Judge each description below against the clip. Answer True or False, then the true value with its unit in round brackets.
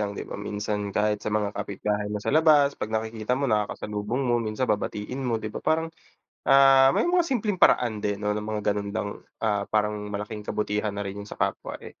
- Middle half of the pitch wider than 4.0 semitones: False (3.5 semitones)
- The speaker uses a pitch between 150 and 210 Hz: False (105 Hz)